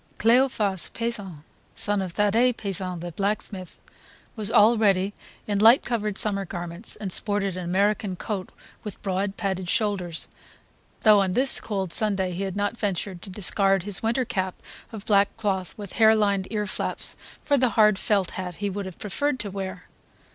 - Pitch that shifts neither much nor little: No, narrow, 2.2 semitones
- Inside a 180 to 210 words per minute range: No, average, 165 wpm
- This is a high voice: Yes, high, 200 Hz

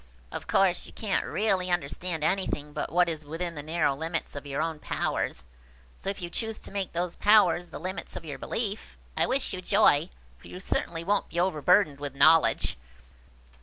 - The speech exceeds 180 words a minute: Yes, average, 190 wpm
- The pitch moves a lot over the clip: No, average, 3.7 semitones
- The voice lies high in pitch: No, medium, 175 Hz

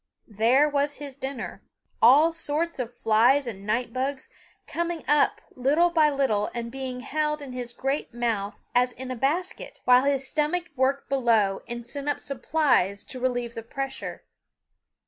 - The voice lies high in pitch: Yes, very high, 265 Hz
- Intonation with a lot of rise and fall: No, average, 3.4 semitones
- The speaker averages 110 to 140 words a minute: No, average, 160 wpm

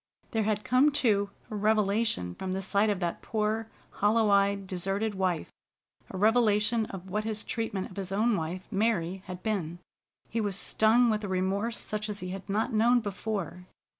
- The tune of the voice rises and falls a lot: No, narrow, 2.4 semitones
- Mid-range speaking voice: No, high, 205 Hz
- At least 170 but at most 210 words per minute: Yes, average, 180 wpm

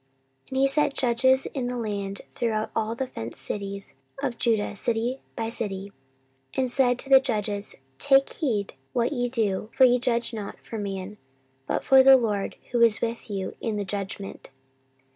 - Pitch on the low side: No, high, 230 Hz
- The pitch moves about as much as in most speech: Yes, average, 3.8 semitones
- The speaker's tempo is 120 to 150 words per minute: No, average, 180 wpm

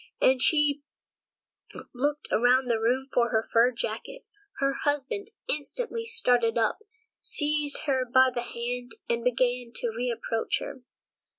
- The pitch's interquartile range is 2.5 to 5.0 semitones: Yes, average, 3.5 semitones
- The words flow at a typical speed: No, slow, 130 wpm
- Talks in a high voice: Yes, very high, 250 Hz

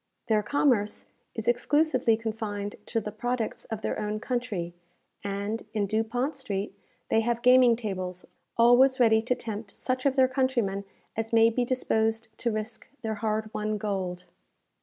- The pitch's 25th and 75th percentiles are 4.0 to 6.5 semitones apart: No, narrow, 2.6 semitones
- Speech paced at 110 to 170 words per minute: Yes, average, 155 wpm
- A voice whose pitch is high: Yes, high, 225 Hz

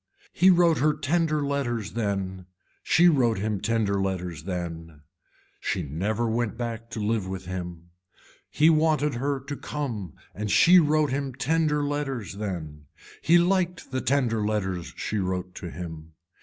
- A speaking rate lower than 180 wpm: Yes, average, 150 wpm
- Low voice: Yes, low, 115 Hz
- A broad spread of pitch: Yes, wide, 7.7 semitones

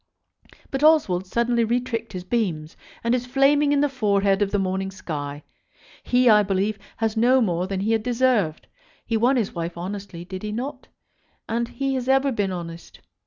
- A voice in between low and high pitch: No, high, 215 Hz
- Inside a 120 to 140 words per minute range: No, average, 180 wpm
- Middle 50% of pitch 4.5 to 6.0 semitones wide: Yes, average, 4.8 semitones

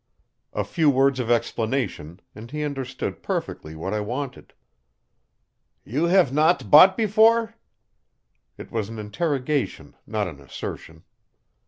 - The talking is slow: Yes, slow, 125 wpm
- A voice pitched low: Yes, low, 130 Hz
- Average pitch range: No, wide, 6.3 semitones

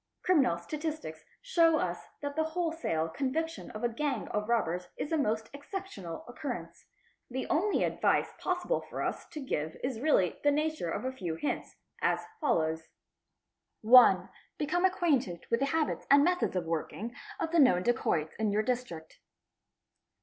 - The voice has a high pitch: Yes, very high, 260 Hz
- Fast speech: No, average, 165 wpm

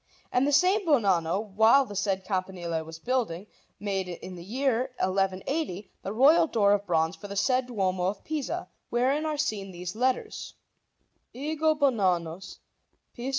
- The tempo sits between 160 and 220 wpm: No, average, 150 wpm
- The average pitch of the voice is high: Yes, high, 205 Hz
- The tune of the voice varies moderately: No, wide, 6.2 semitones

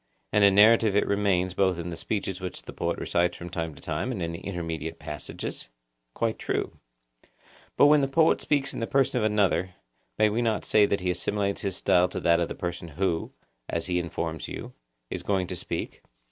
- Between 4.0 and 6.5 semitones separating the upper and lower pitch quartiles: No, average, 3.5 semitones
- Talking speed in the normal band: No, fast, 210 wpm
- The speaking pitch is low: Yes, very low, 95 Hz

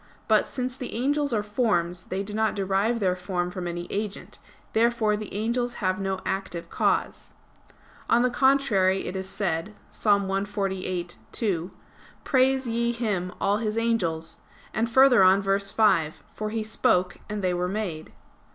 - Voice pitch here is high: Yes, high, 205 Hz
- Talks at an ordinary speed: Yes, average, 155 wpm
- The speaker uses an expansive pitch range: No, average, 3.7 semitones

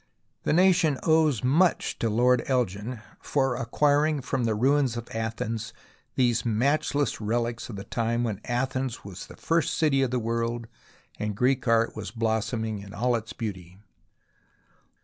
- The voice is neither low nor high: No, low, 120 Hz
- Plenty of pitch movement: No, average, 3.2 semitones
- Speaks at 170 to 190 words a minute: No, average, 150 wpm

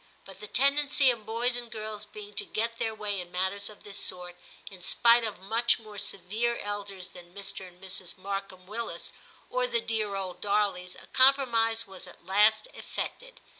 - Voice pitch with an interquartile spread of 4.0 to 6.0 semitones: No, average, 3.6 semitones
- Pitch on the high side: Yes, high, 210 Hz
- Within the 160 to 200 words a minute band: Yes, average, 180 wpm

